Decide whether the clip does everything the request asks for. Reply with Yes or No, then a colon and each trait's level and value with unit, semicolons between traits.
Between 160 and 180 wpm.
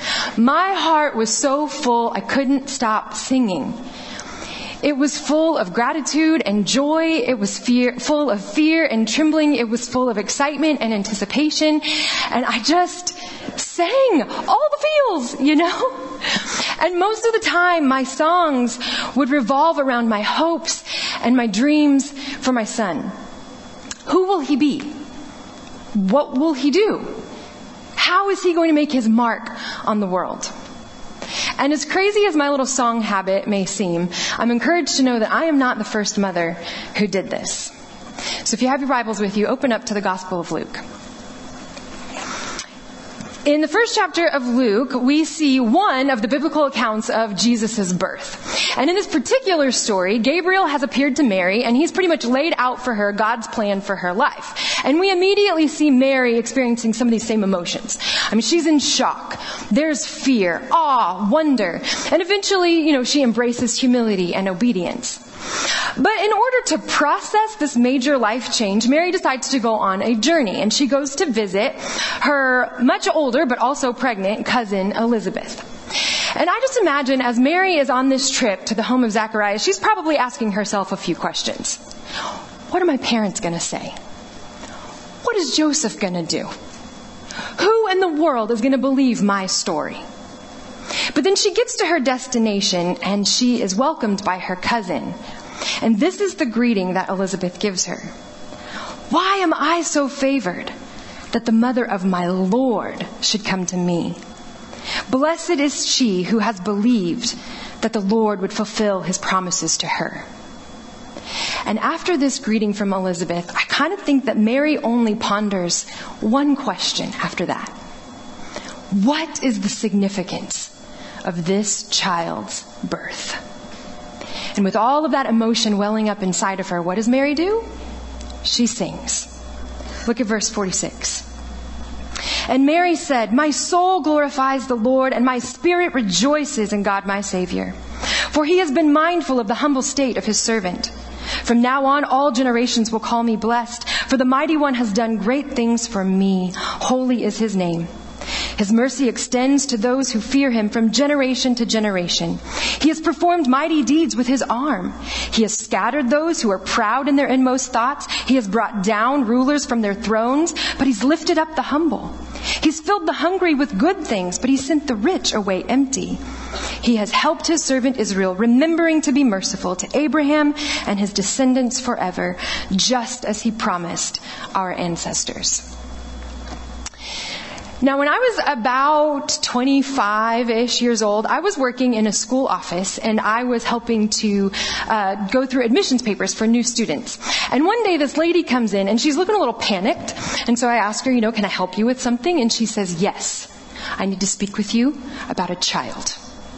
Yes: average, 170 wpm